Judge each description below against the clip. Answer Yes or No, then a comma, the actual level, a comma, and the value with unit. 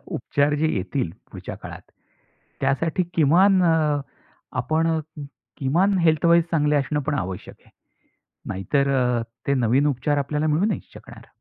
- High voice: No, medium, 150 Hz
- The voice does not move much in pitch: No, average, 3.1 semitones